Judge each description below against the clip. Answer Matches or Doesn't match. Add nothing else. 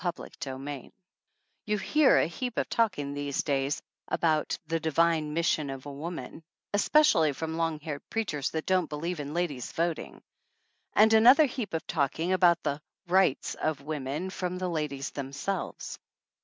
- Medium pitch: Matches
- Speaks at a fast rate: Doesn't match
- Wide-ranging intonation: Doesn't match